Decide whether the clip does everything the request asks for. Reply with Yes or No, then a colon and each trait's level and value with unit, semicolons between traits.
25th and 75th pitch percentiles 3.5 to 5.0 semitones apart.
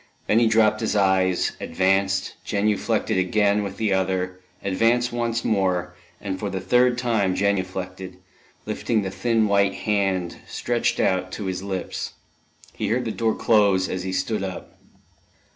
No: average, 2.8 semitones